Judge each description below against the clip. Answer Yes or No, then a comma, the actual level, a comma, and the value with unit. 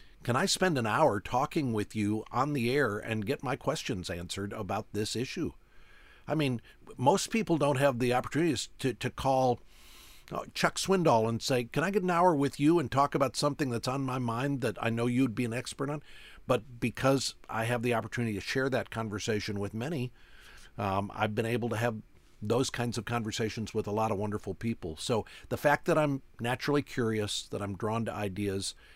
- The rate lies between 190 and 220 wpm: Yes, average, 200 wpm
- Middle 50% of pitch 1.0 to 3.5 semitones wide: No, average, 4.4 semitones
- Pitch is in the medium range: No, low, 120 Hz